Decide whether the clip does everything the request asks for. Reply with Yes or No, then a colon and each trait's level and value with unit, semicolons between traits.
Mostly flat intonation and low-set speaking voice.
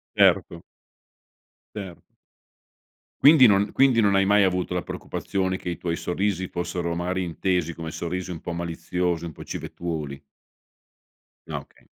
Yes: narrow, 2.3 semitones; very low, 90 Hz